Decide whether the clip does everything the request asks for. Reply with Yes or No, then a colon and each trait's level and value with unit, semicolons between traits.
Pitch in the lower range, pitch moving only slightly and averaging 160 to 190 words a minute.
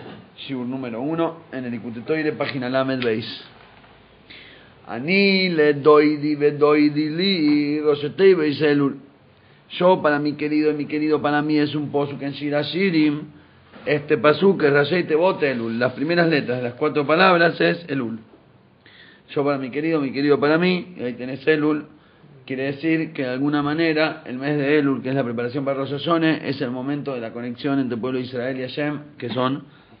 No: medium, 150 Hz; narrow, 2.2 semitones; average, 175 wpm